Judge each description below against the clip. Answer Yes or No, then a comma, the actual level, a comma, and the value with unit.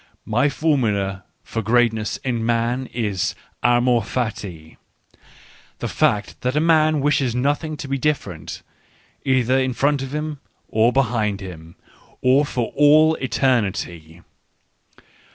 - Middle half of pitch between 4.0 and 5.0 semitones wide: Yes, average, 4.7 semitones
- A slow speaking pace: Yes, slow, 120 wpm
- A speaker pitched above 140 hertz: No, low, 125 Hz